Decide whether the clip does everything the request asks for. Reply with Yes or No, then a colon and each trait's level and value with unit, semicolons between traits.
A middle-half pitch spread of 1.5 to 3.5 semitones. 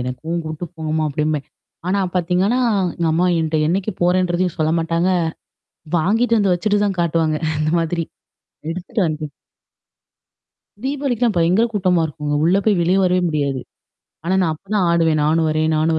Yes: average, 2.9 semitones